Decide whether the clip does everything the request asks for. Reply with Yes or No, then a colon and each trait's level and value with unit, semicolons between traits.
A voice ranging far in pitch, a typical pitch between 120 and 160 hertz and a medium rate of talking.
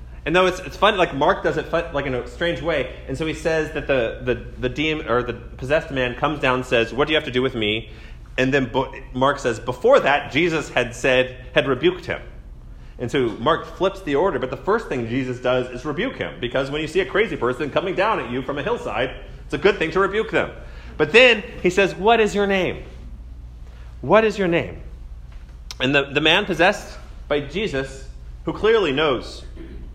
No: wide, 6.3 semitones; low, 135 Hz; fast, 220 wpm